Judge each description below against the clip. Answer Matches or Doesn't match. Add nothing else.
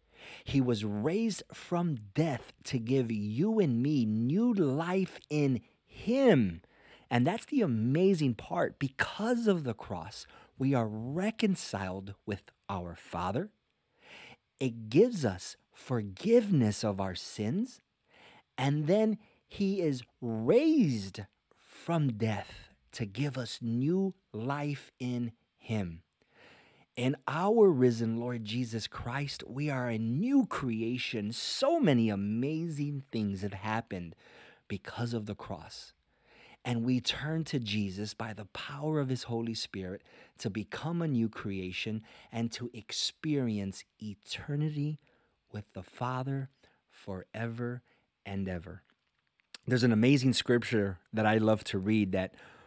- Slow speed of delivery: Matches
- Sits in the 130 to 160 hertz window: Doesn't match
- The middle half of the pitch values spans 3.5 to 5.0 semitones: Doesn't match